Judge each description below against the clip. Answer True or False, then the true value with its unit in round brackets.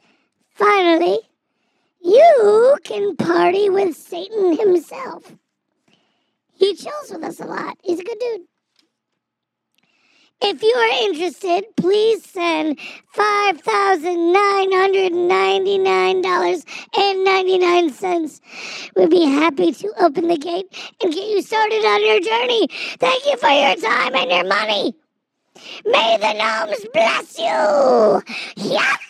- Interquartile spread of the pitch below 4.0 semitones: True (3.3 semitones)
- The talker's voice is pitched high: True (370 Hz)